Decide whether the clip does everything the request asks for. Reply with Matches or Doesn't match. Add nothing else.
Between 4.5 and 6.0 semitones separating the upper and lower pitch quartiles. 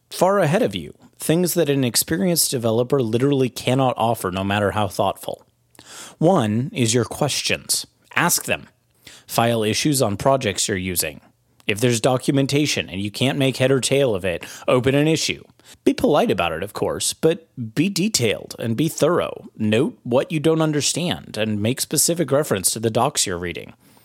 Matches